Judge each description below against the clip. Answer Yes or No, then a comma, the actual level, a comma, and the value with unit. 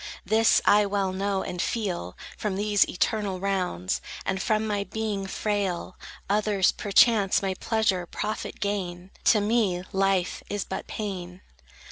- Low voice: No, high, 195 Hz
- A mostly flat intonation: Yes, narrow, 2.1 semitones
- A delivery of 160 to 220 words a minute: No, slow, 135 wpm